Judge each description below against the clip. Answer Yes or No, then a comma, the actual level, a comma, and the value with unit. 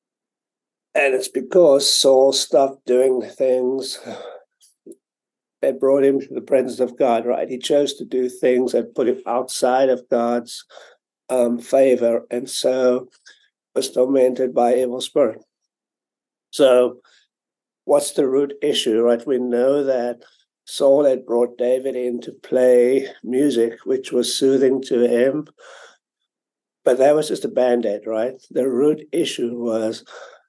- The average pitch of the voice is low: Yes, low, 125 Hz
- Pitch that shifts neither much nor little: No, narrow, 1.7 semitones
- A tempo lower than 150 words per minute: Yes, average, 140 wpm